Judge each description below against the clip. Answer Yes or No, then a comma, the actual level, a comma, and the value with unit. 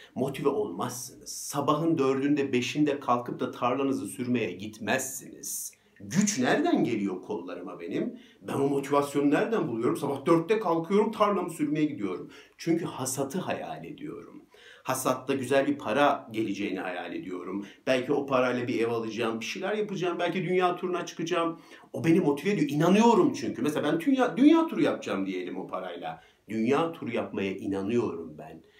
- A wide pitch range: Yes, wide, 6.1 semitones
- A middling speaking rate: No, fast, 145 wpm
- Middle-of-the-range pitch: Yes, medium, 145 Hz